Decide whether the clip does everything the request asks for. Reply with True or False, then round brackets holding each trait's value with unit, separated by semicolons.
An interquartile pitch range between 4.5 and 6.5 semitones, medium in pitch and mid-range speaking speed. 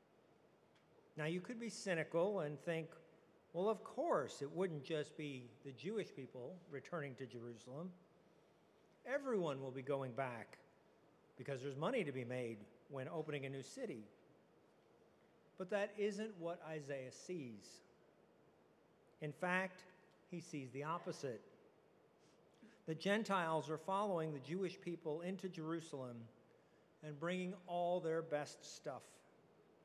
False (4.8 semitones; 160 Hz; 125 wpm)